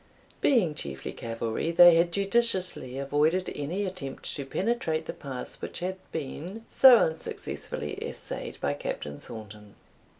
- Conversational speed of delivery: No, slow, 130 wpm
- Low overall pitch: No, medium, 160 Hz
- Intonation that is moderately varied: No, wide, 6.5 semitones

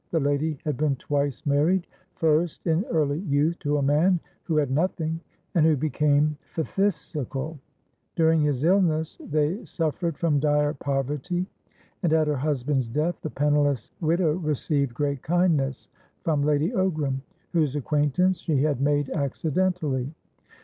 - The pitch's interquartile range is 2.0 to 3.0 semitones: Yes, narrow, 2.4 semitones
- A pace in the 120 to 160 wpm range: Yes, average, 140 wpm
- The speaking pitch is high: No, medium, 150 Hz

